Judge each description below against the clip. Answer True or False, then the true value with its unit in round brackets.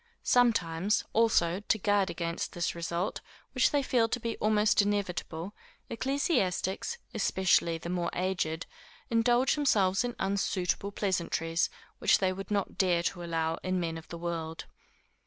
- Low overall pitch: False (185 Hz)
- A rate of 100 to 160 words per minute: True (140 wpm)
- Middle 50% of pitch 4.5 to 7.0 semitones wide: False (4.0 semitones)